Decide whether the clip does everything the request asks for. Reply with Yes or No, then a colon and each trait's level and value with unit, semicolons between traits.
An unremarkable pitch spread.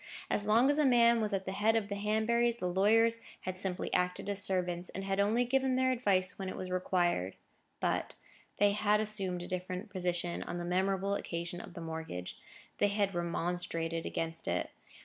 Yes: average, 3.2 semitones